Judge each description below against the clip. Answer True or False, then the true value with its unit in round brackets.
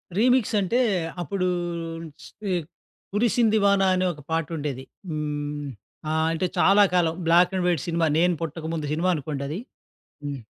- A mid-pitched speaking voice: True (165 Hz)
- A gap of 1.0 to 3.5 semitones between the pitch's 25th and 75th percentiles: False (4.1 semitones)